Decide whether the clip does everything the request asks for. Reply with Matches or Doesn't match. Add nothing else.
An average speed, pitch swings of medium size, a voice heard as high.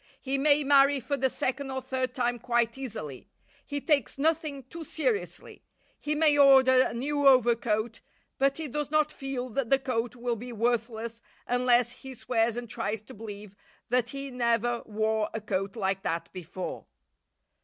Matches